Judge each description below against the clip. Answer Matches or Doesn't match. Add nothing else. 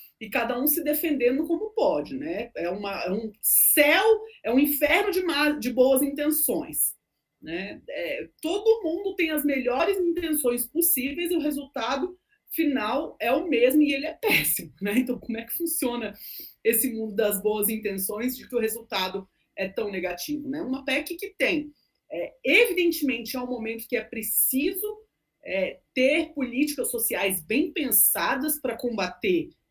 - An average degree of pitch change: Doesn't match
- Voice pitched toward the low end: Doesn't match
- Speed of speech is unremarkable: Matches